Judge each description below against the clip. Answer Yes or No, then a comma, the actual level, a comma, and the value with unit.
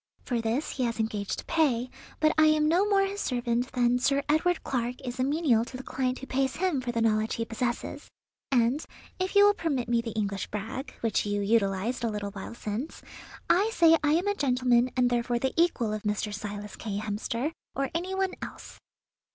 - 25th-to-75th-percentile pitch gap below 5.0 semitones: No, average, 5.3 semitones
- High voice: Yes, very high, 250 Hz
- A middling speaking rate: No, fast, 210 wpm